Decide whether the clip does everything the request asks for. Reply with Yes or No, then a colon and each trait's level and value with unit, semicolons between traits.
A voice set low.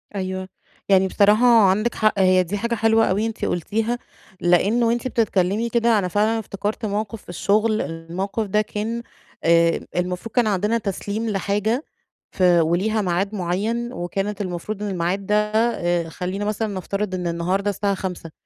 No: high, 200 Hz